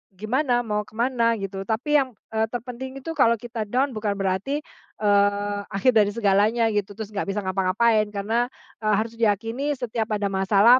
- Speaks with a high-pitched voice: Yes, high, 220 Hz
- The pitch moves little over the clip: No, average, 3.0 semitones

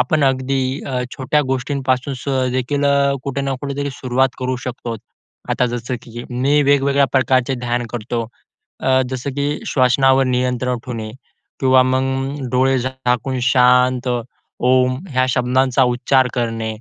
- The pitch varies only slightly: Yes, narrow, 1.3 semitones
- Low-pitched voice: Yes, low, 130 Hz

